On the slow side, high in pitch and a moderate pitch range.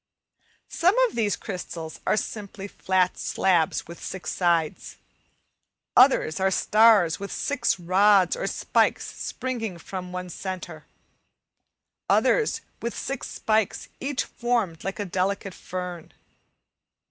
Yes: slow, 115 wpm; high, 195 Hz; average, 3.7 semitones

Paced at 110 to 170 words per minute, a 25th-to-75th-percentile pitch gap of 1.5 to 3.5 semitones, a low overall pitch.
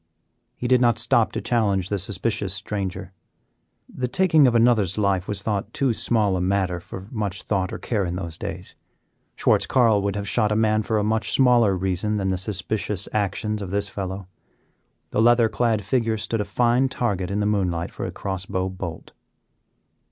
No: average, 190 wpm; average, 2.9 semitones; low, 105 Hz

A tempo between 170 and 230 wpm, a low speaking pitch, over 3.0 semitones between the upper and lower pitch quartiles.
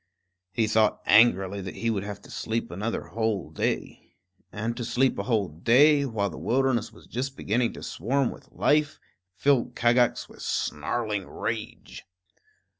No: average, 155 wpm; low, 115 Hz; average, 3.5 semitones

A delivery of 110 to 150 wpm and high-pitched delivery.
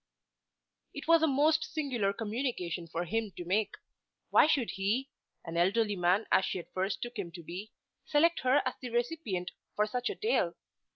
No: average, 180 wpm; high, 220 Hz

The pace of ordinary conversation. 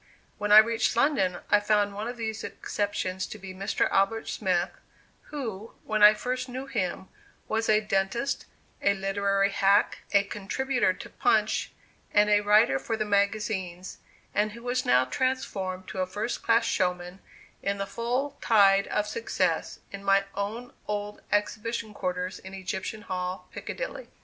Yes: average, 155 wpm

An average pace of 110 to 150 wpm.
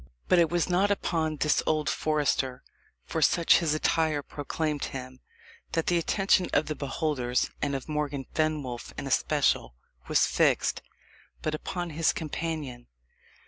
Yes: average, 140 wpm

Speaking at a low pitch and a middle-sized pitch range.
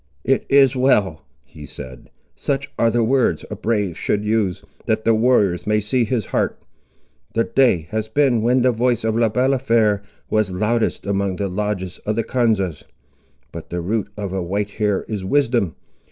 Yes: low, 110 Hz; average, 3.4 semitones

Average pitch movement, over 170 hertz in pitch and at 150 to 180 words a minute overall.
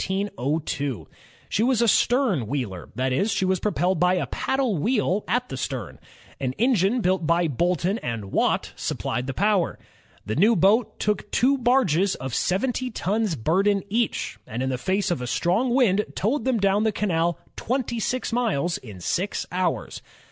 No: wide, 6.4 semitones; high, 190 Hz; average, 165 wpm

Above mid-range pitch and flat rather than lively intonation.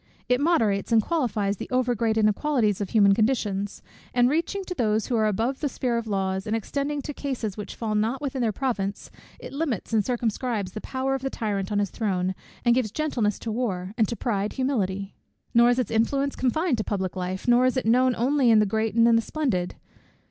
No: high, 230 Hz; average, 3.9 semitones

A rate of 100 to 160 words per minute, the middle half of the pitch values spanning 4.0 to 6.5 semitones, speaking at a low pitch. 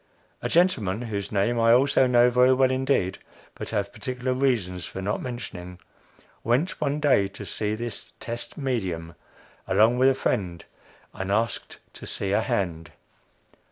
Yes: average, 155 wpm; average, 4.8 semitones; low, 115 Hz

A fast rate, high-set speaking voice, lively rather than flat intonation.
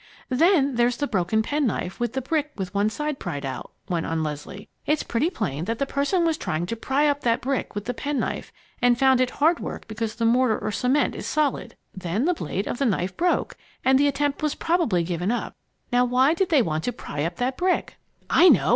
Yes: fast, 225 wpm; high, 245 Hz; wide, 6.3 semitones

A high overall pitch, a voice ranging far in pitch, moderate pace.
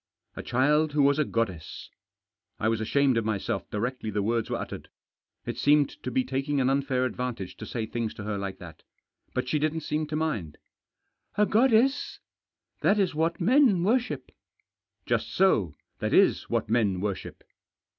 No: low, 130 Hz; wide, 6.1 semitones; average, 180 wpm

